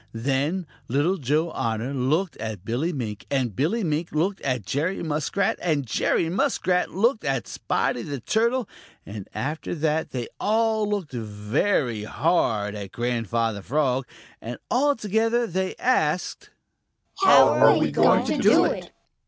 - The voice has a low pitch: No, medium, 150 Hz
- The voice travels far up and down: Yes, wide, 8.0 semitones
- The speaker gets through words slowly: No, average, 145 wpm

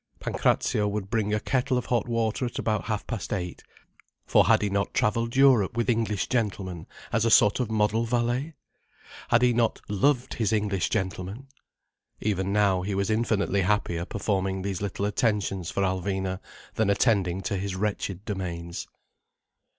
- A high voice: No, low, 105 Hz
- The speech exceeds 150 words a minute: Yes, average, 160 wpm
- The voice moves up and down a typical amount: Yes, average, 3.1 semitones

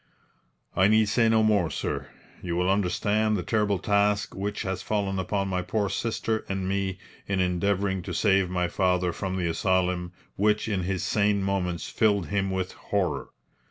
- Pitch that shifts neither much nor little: No, narrow, 2.0 semitones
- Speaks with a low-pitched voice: Yes, very low, 95 Hz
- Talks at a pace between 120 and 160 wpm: No, average, 170 wpm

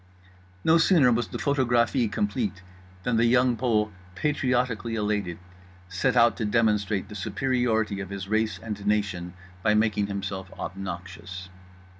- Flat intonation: No, average, 3.3 semitones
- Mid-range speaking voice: No, low, 105 Hz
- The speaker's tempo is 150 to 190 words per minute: No, slow, 135 wpm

